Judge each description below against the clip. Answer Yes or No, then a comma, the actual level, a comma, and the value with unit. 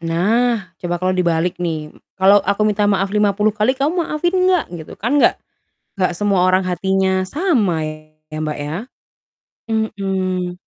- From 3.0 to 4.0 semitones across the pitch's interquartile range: Yes, average, 3.3 semitones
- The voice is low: No, high, 190 Hz